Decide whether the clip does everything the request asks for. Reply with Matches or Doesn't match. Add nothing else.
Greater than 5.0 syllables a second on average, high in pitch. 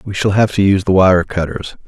Doesn't match